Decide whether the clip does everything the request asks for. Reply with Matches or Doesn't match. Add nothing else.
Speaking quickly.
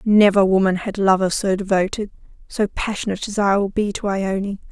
Doesn't match